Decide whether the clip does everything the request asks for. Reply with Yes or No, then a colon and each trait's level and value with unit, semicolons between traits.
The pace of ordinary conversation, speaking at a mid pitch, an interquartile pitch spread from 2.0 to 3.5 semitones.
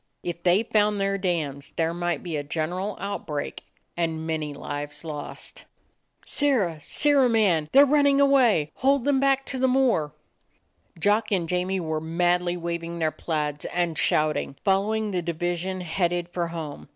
No: average, 160 wpm; medium, 175 Hz; average, 4.8 semitones